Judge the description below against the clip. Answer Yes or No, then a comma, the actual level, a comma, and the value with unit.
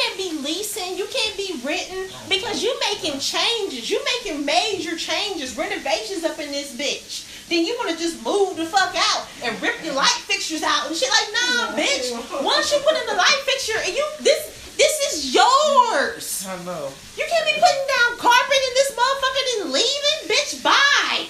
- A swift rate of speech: No, average, 190 wpm